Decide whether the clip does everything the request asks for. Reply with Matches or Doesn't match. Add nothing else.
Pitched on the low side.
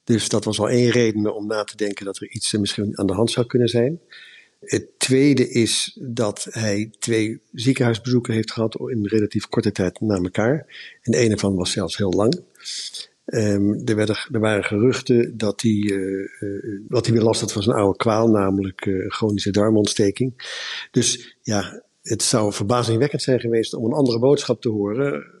Matches